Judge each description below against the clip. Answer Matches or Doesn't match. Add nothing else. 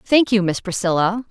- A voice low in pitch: Doesn't match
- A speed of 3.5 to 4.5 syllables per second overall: Doesn't match